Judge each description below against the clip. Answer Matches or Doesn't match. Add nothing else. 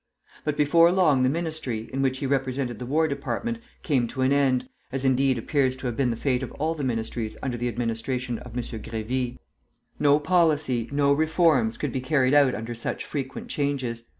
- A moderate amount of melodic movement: Matches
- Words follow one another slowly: Doesn't match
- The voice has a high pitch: Doesn't match